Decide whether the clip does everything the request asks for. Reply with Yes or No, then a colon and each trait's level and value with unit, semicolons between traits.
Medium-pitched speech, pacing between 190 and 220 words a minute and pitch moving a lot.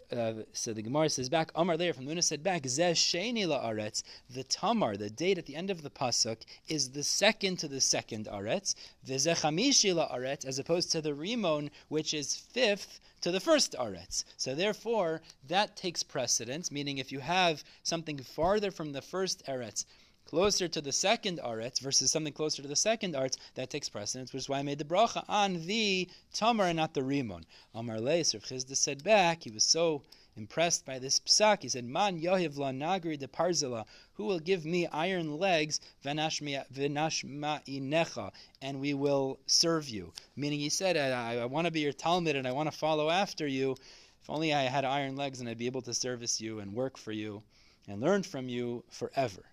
No: medium, 145 Hz; average, 195 wpm; average, 4.8 semitones